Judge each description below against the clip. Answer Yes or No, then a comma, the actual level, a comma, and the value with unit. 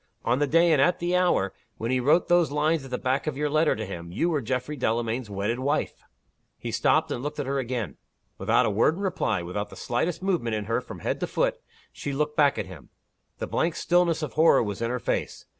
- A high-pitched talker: No, low, 135 Hz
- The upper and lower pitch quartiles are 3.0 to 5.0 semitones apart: No, wide, 5.6 semitones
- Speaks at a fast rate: Yes, fast, 240 wpm